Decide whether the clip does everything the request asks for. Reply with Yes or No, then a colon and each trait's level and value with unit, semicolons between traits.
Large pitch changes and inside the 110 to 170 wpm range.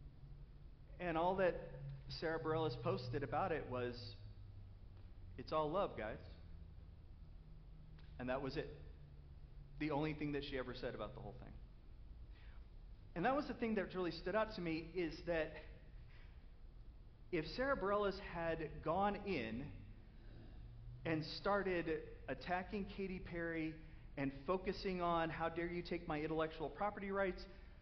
Yes: wide, 8.4 semitones; slow, 135 wpm